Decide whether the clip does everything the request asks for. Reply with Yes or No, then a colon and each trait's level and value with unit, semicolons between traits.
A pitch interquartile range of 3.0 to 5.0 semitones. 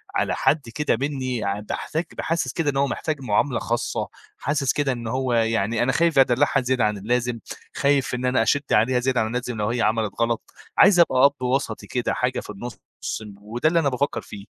Yes: average, 3.6 semitones